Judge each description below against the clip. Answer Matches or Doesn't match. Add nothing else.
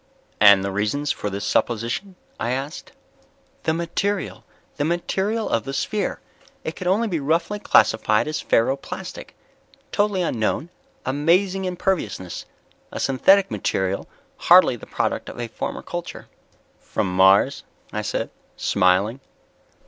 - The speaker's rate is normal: Doesn't match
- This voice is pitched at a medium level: Matches